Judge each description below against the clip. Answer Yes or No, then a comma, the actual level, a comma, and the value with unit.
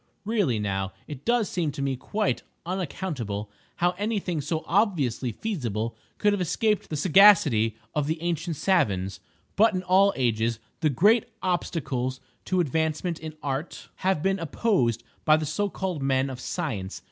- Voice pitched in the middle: Yes, medium, 160 Hz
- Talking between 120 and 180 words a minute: Yes, average, 160 wpm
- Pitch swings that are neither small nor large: No, wide, 6.9 semitones